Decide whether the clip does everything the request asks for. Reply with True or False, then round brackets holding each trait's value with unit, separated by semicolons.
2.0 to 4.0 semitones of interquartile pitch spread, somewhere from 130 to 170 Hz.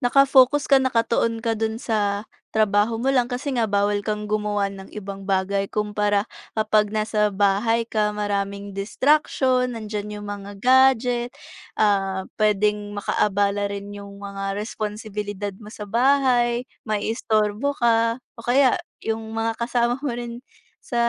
False (2.8 semitones; 215 Hz)